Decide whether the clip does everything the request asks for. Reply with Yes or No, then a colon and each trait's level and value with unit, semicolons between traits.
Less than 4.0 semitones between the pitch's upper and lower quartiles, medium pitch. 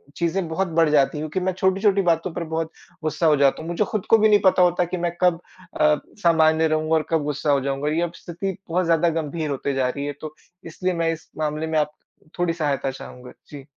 Yes: average, 2.7 semitones; medium, 160 Hz